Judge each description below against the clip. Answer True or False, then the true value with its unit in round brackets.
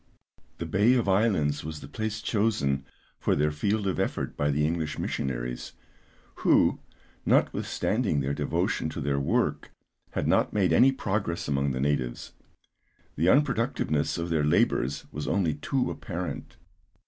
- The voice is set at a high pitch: False (80 Hz)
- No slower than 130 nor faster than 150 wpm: True (145 wpm)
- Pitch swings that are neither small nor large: False (6.6 semitones)